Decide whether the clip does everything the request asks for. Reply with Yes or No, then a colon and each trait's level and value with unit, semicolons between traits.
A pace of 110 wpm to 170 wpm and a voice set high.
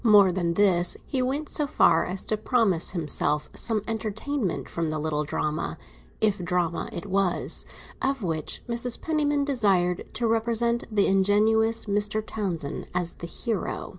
Yes: average, 140 wpm; high, 205 Hz